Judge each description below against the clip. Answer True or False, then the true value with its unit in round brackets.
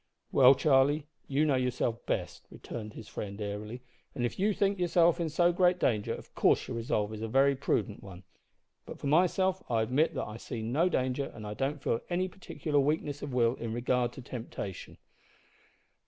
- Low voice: True (130 Hz)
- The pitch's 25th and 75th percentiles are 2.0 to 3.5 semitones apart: False (5.5 semitones)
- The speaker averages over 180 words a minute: True (190 wpm)